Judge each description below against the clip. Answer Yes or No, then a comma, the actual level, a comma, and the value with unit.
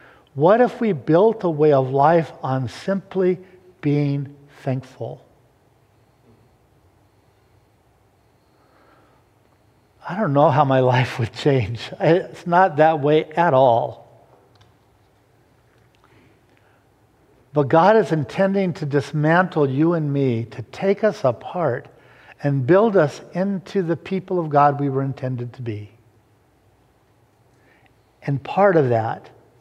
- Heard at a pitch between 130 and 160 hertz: Yes, low, 135 Hz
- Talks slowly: Yes, slow, 115 wpm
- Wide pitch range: Yes, wide, 5.8 semitones